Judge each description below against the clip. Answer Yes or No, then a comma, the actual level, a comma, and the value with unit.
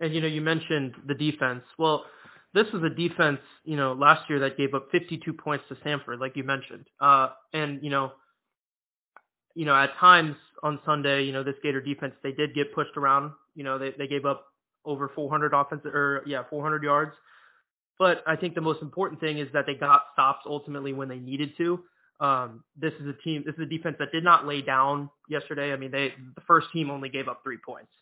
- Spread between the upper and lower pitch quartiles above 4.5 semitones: No, narrow, 2.4 semitones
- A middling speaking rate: No, fast, 220 wpm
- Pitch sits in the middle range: Yes, medium, 145 Hz